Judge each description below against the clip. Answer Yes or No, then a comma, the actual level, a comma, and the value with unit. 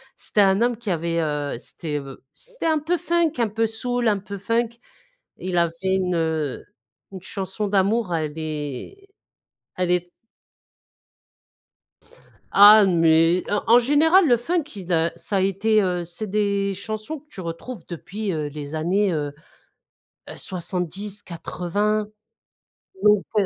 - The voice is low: No, high, 195 Hz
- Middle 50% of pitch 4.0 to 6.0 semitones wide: Yes, average, 4.5 semitones